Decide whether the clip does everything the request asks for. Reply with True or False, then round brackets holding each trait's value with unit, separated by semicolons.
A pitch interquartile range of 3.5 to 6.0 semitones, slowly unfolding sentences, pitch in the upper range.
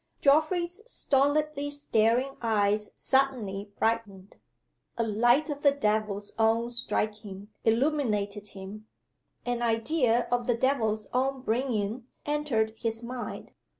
True (4.2 semitones; 110 wpm; 235 Hz)